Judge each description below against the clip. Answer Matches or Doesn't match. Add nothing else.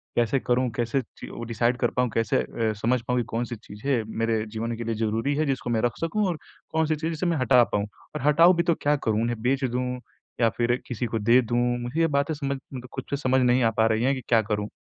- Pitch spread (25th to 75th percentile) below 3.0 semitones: Doesn't match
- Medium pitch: Doesn't match